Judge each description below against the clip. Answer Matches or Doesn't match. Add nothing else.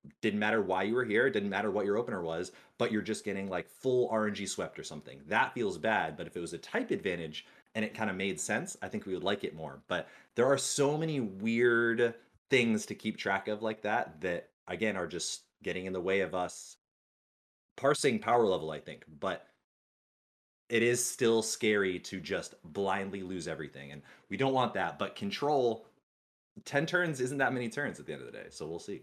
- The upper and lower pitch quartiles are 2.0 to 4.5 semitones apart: Doesn't match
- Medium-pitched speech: Doesn't match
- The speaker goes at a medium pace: Doesn't match